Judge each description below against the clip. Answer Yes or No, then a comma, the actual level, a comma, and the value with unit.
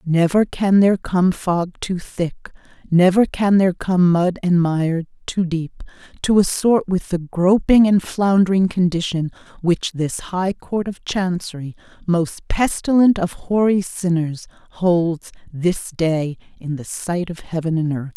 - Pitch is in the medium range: Yes, medium, 180 Hz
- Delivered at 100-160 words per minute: Yes, average, 150 wpm